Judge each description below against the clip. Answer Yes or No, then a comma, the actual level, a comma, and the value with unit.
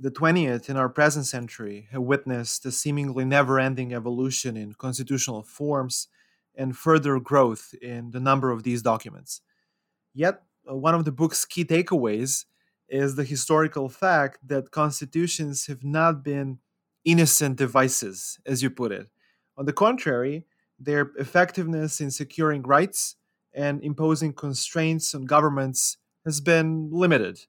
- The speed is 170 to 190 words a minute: No, average, 140 wpm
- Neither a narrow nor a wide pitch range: Yes, average, 3.3 semitones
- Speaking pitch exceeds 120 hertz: Yes, medium, 140 Hz